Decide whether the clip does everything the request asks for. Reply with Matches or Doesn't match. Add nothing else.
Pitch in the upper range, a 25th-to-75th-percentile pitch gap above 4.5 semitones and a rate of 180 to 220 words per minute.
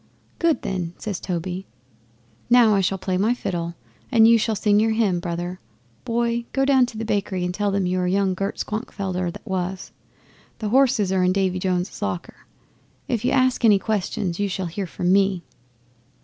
Doesn't match